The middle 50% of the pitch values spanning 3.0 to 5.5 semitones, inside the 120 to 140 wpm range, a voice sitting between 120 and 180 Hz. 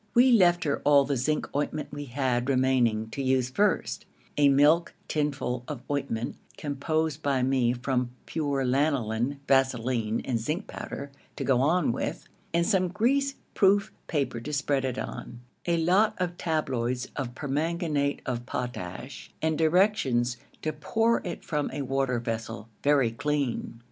No: average, 4.1 semitones; average, 150 wpm; medium, 140 Hz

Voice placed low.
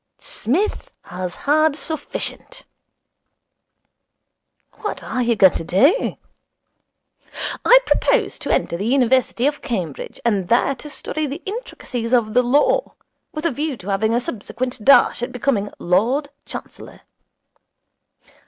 No: very high, 250 Hz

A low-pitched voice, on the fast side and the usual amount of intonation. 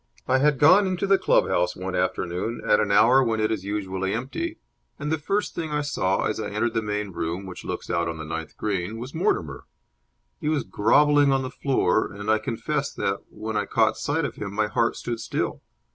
No: low, 110 Hz; fast, 220 wpm; wide, 6.2 semitones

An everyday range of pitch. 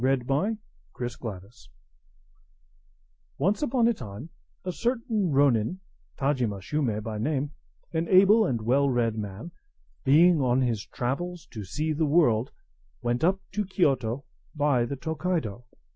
No: wide, 6.7 semitones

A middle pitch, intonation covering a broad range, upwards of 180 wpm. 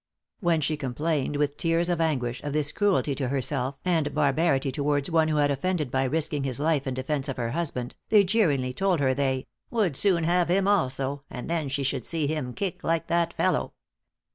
No: medium, 150 Hz; average, 3.8 semitones; average, 200 wpm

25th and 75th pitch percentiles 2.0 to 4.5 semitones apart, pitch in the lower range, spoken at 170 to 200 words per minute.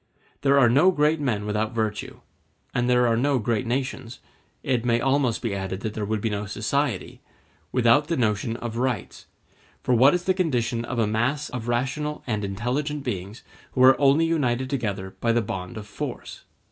Yes: average, 3.9 semitones; low, 120 Hz; average, 180 wpm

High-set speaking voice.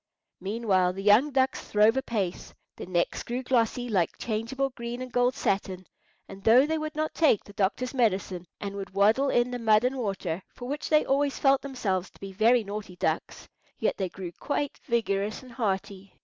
Yes: high, 225 Hz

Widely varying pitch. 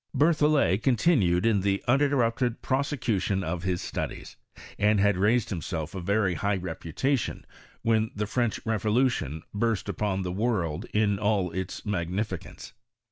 No: average, 4.1 semitones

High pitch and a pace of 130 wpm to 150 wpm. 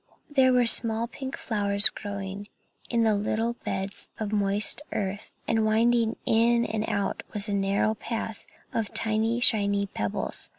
Yes: high, 215 Hz; average, 140 wpm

